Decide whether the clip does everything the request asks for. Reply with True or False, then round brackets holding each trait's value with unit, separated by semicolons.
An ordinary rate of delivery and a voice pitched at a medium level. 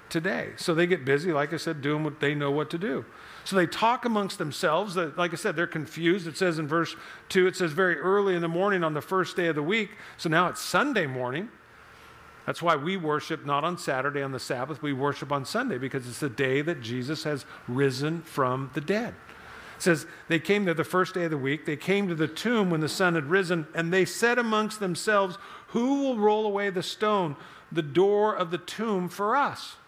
False (225 wpm; 170 Hz)